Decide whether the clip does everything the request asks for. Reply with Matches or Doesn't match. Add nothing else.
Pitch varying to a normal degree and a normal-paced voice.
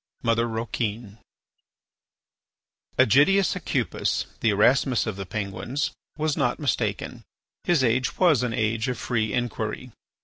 Doesn't match